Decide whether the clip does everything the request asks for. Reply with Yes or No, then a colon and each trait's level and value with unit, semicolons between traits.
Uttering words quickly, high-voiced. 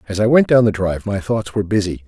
No: fast, 290 wpm; low, 105 Hz